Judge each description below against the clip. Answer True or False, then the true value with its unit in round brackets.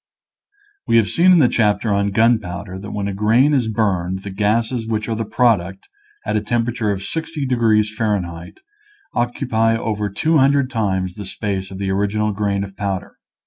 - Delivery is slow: False (175 wpm)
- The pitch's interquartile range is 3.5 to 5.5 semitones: False (2.9 semitones)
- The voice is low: True (105 Hz)